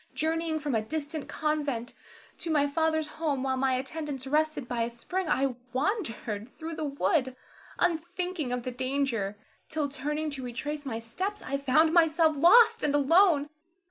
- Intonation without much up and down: No, average, 3.5 semitones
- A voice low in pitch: No, very high, 290 Hz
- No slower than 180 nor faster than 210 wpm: No, average, 160 wpm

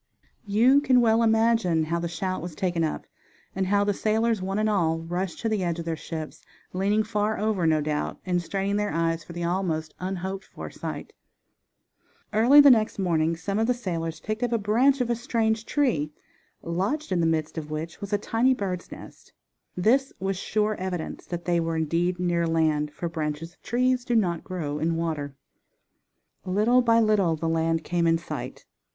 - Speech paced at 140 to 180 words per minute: No, average, 195 wpm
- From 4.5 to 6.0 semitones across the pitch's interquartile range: Yes, average, 4.8 semitones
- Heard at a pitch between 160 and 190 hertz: Yes, medium, 185 Hz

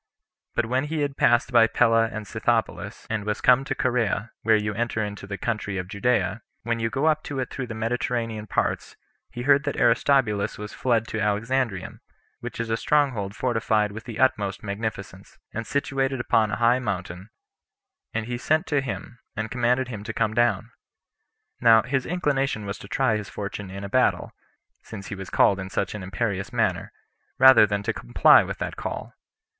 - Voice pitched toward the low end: Yes, low, 115 Hz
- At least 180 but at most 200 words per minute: Yes, average, 190 wpm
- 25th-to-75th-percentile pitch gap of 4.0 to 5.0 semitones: No, average, 3.4 semitones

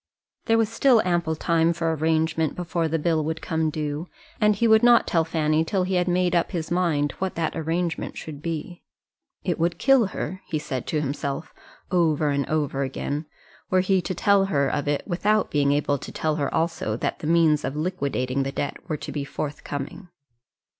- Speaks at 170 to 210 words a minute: Yes, average, 195 wpm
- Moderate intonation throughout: Yes, average, 3.4 semitones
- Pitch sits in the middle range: Yes, medium, 160 Hz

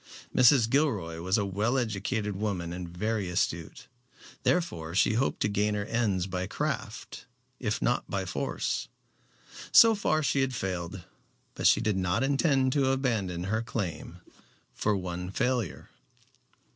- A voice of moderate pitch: No, low, 105 Hz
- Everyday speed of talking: Yes, average, 145 wpm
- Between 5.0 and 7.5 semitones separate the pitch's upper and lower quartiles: Yes, wide, 5.6 semitones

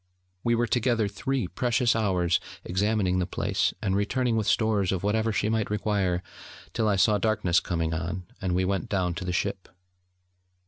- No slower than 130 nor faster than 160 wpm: No, average, 175 wpm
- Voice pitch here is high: No, low, 100 Hz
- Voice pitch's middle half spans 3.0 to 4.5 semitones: Yes, average, 3.3 semitones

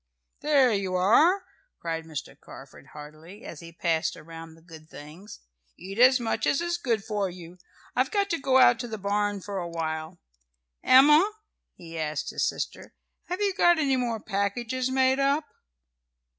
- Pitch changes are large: Yes, wide, 7.9 semitones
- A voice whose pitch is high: Yes, high, 205 Hz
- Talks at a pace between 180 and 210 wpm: No, average, 170 wpm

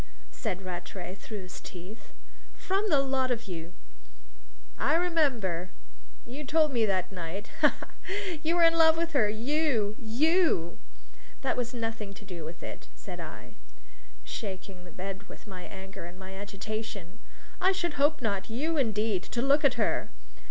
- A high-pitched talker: Yes, high, 220 Hz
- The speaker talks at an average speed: Yes, average, 165 wpm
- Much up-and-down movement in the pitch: Yes, wide, 7.7 semitones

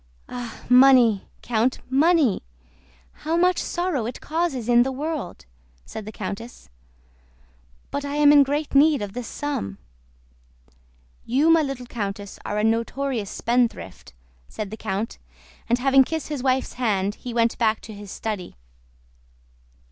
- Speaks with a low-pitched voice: No, high, 245 Hz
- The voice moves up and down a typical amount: Yes, average, 4.6 semitones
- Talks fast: No, average, 140 wpm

